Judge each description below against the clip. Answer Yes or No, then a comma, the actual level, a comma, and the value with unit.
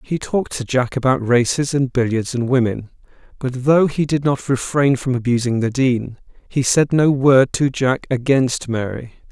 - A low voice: Yes, low, 130 Hz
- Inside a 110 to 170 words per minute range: No, average, 180 wpm